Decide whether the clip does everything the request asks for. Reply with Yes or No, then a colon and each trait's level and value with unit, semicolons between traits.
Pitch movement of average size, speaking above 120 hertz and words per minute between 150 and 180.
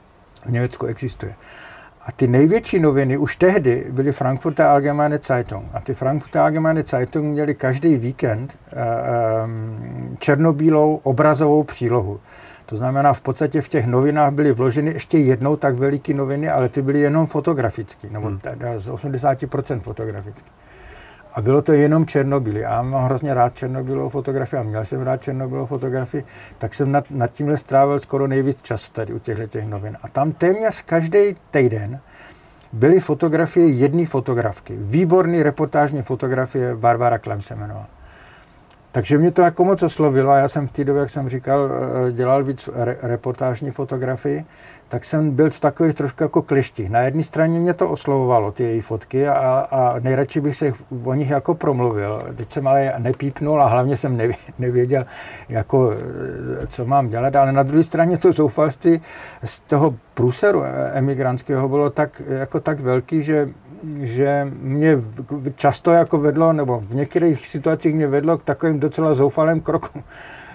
Yes: average, 3.4 semitones; medium, 140 Hz; average, 155 wpm